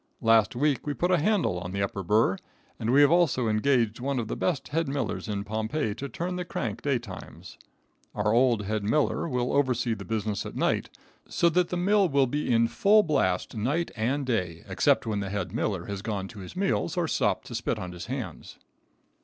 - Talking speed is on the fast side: Yes, fast, 210 wpm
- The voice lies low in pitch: Yes, low, 120 Hz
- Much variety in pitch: Yes, wide, 6.0 semitones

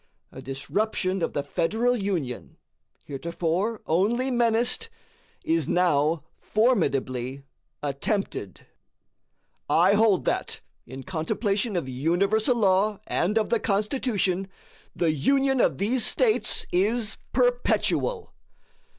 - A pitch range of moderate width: No, wide, 6.3 semitones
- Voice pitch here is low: No, high, 200 Hz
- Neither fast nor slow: No, slow, 100 wpm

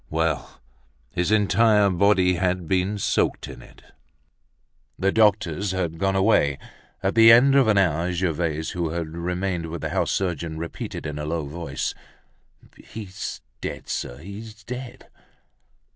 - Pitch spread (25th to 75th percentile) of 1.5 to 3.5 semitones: No, average, 3.9 semitones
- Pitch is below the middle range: Yes, very low, 90 Hz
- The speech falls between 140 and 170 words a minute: Yes, average, 145 wpm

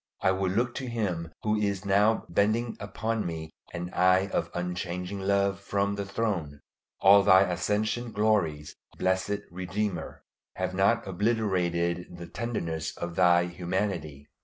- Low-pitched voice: Yes, very low, 95 Hz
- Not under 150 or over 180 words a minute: No, slow, 135 wpm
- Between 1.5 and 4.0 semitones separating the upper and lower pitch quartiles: Yes, average, 3.0 semitones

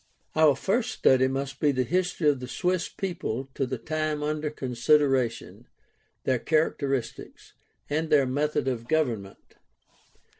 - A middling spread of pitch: Yes, average, 3.2 semitones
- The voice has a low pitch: No, medium, 145 Hz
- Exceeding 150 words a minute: No, slow, 135 wpm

